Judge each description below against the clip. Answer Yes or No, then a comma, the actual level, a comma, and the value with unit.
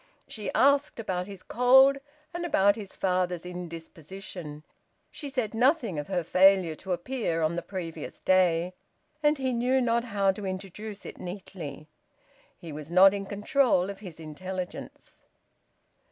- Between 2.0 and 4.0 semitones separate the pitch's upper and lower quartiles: No, average, 4.7 semitones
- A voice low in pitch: No, high, 190 Hz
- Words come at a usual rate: Yes, average, 145 wpm